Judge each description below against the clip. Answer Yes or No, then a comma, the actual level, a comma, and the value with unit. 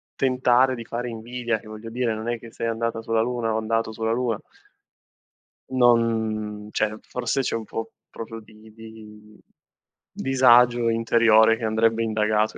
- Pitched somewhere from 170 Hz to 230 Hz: No, low, 115 Hz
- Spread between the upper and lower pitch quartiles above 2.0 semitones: No, narrow, 1.4 semitones